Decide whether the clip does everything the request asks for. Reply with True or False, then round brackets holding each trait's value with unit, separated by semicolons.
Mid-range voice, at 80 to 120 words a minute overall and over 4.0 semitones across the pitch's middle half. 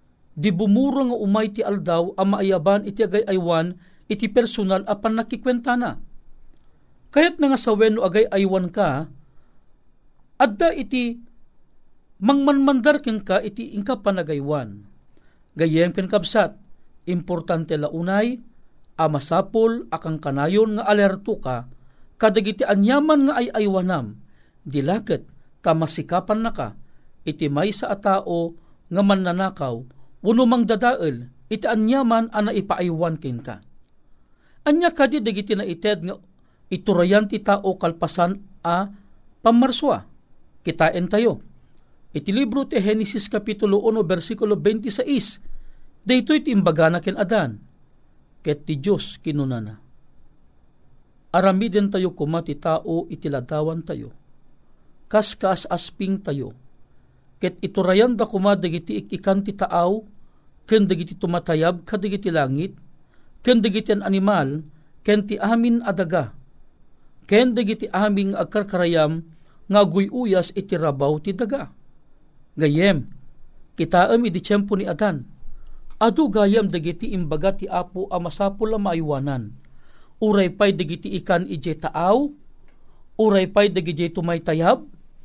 False (195 Hz; 115 wpm; 4.7 semitones)